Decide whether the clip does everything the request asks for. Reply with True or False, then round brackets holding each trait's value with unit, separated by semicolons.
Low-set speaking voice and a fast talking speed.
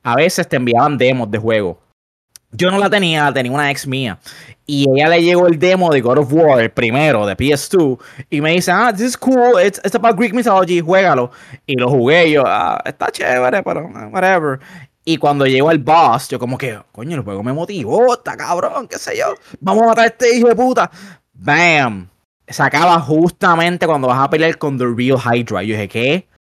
False (155 Hz; 215 wpm)